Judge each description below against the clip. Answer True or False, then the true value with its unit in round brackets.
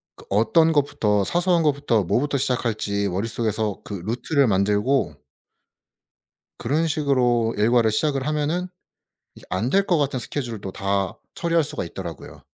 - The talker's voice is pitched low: True (120 Hz)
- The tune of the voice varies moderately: False (5.9 semitones)